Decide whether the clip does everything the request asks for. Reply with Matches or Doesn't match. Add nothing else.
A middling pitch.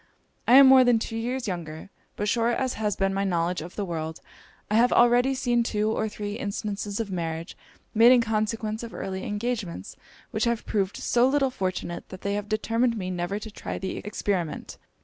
Doesn't match